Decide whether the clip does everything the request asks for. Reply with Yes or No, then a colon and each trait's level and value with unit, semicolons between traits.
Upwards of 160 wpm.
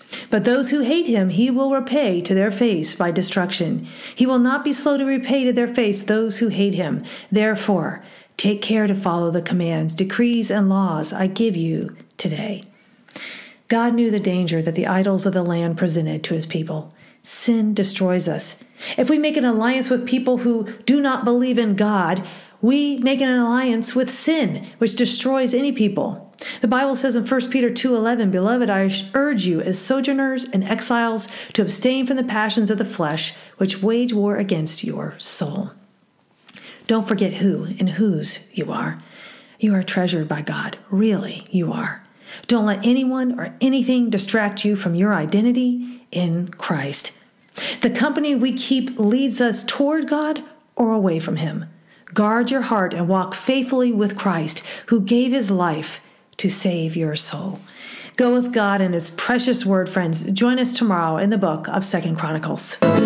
Yes: average, 175 wpm